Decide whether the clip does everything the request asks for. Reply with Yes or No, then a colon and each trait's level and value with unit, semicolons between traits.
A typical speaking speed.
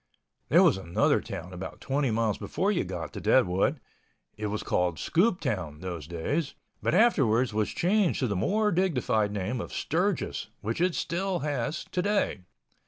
Yes: average, 160 wpm